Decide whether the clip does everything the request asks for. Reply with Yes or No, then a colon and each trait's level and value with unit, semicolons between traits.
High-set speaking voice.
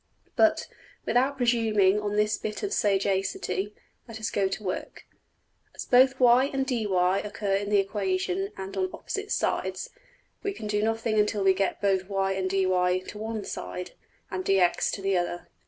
Yes: high, 210 Hz